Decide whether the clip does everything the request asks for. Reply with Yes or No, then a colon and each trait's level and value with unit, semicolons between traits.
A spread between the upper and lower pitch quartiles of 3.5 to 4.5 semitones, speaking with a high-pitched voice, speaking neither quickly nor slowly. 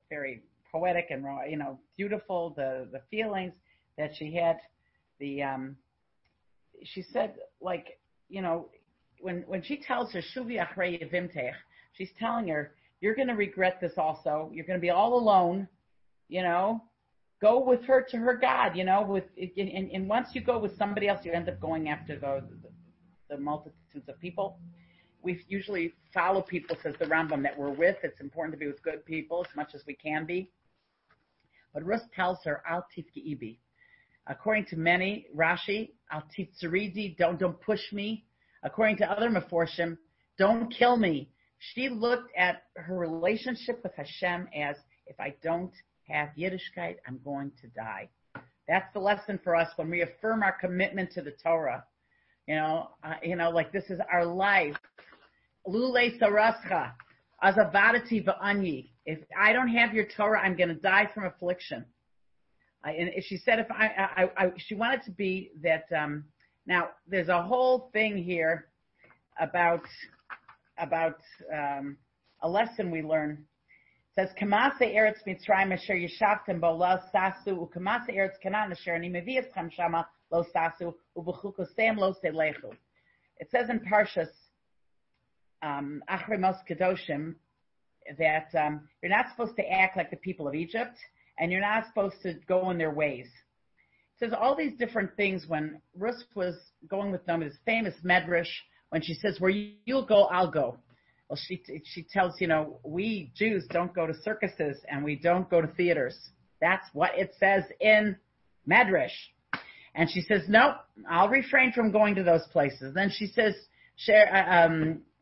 No: average, 4.1 semitones; medium, 180 Hz; average, 160 wpm